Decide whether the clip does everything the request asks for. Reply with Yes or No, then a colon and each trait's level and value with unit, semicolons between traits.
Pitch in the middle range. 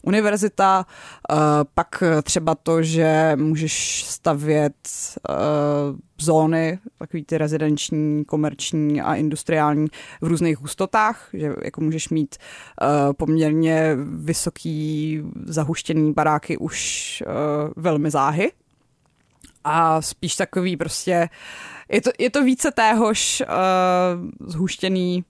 Yes: medium, 160 Hz